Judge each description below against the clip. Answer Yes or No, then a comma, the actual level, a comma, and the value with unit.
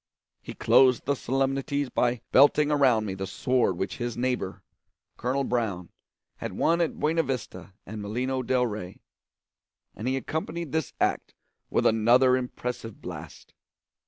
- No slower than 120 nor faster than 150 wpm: Yes, average, 140 wpm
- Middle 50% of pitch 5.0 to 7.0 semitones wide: No, average, 3.5 semitones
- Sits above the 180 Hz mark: No, low, 125 Hz